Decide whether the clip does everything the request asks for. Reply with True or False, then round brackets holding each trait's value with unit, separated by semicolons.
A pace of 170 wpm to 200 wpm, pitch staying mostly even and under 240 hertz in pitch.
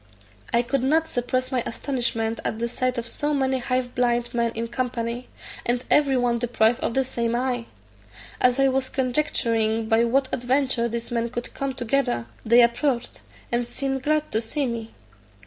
False (175 wpm; 2.1 semitones; 245 Hz)